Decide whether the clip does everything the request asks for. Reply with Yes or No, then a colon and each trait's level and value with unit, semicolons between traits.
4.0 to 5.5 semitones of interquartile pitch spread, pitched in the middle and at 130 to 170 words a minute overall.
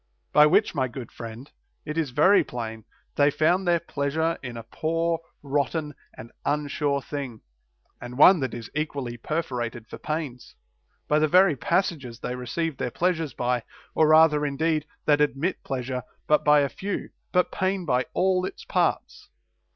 Yes: average, 4.5 semitones; medium, 150 Hz; average, 160 wpm